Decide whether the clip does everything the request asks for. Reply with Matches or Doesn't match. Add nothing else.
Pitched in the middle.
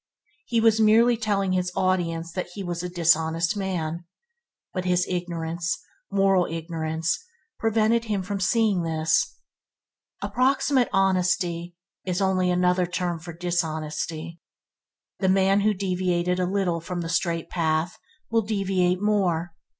Matches